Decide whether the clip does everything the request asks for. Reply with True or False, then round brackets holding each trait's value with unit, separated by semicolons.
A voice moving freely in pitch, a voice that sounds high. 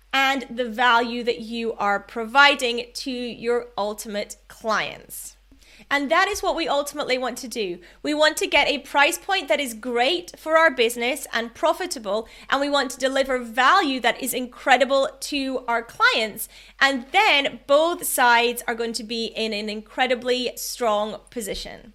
False (3.4 semitones; 255 Hz)